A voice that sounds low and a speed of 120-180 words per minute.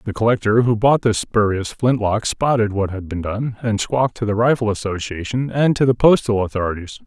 No: low, 110 Hz; average, 195 wpm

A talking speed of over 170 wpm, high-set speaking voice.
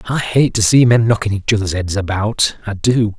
No: fast, 205 wpm; low, 110 Hz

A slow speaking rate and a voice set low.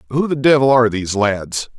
No: average, 200 wpm; low, 120 Hz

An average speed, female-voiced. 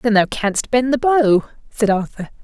Yes: average, 195 wpm; female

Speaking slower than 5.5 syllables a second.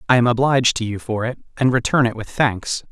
No: 6.0 syllables/s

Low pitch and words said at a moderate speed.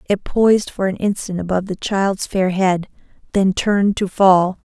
No: high, 195 Hz; average, 165 wpm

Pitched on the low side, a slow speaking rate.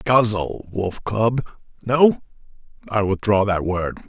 Yes: low, 105 Hz; slow, 120 wpm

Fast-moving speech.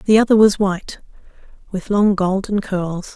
No: average, 150 wpm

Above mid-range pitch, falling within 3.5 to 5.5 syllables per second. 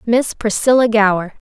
Yes: high, 220 Hz; 4.7 syllables/s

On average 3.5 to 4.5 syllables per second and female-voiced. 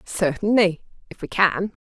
Yes: 4.3 syllables/s; female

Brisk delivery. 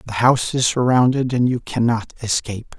No: average, 170 wpm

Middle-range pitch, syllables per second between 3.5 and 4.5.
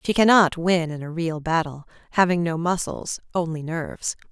No: medium, 170 Hz; 5.0 syllables/s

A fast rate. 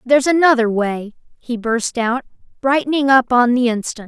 No: average, 160 wpm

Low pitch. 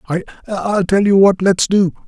No: high, 190 Hz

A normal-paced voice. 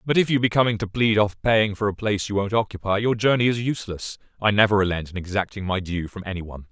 No: fast, 260 wpm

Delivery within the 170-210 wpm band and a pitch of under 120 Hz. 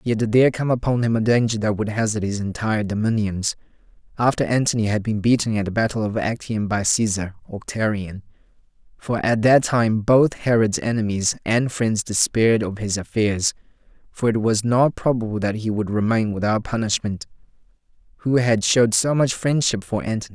Yes: average, 175 wpm; low, 110 Hz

